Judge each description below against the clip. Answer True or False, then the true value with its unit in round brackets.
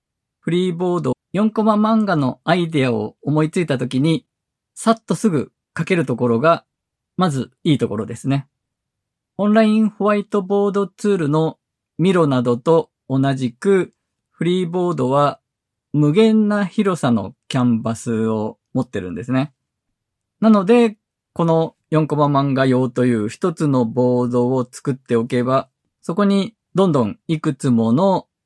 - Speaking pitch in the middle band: True (145 Hz)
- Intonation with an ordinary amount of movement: False (6.9 semitones)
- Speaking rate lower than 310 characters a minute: True (285 characters per minute)